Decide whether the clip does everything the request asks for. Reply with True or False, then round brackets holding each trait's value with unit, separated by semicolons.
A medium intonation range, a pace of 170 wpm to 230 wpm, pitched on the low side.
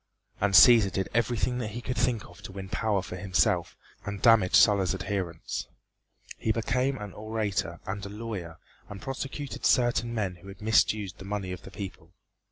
True (3.2 semitones; 175 wpm; 100 Hz)